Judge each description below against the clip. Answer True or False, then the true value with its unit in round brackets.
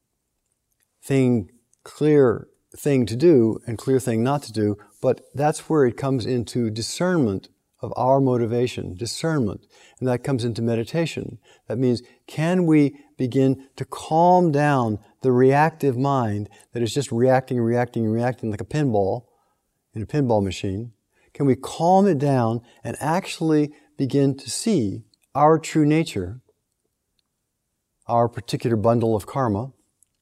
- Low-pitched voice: True (125 Hz)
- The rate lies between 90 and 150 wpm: True (135 wpm)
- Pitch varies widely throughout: False (3.8 semitones)